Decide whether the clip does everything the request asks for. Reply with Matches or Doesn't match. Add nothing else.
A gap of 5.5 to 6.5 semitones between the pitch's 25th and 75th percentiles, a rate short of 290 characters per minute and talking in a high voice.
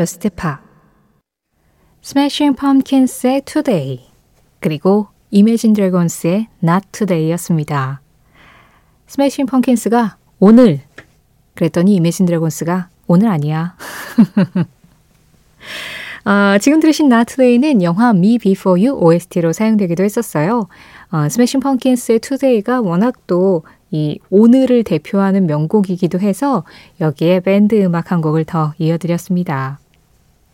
Matches